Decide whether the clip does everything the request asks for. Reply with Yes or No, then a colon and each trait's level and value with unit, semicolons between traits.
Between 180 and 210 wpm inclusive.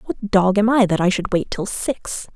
No: fast, 255 wpm